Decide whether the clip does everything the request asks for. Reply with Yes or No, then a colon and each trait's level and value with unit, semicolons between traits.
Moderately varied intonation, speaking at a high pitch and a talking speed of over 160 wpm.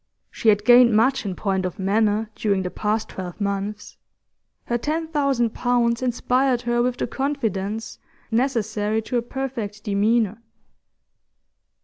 No: average, 3.0 semitones; high, 225 Hz; slow, 135 wpm